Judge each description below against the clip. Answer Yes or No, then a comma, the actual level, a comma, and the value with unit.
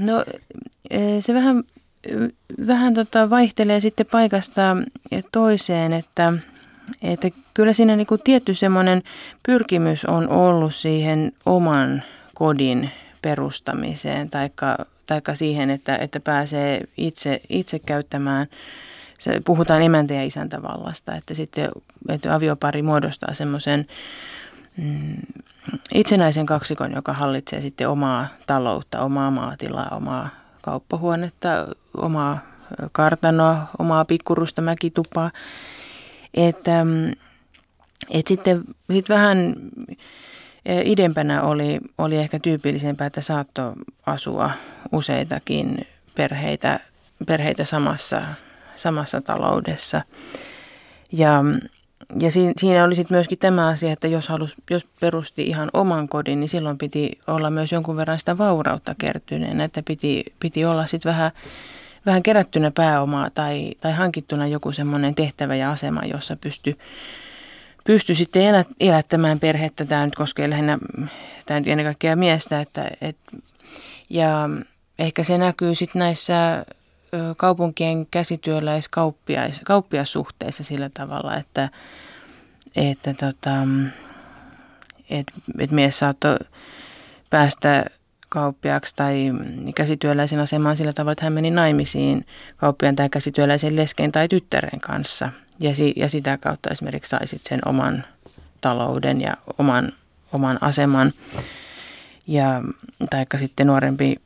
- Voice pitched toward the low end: No, medium, 155 Hz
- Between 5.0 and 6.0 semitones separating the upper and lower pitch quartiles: No, average, 3.5 semitones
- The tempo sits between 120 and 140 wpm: No, average, 110 wpm